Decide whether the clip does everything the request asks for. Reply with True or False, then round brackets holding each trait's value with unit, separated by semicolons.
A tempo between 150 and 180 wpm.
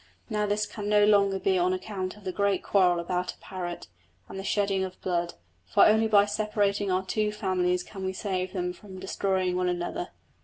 False (200 wpm)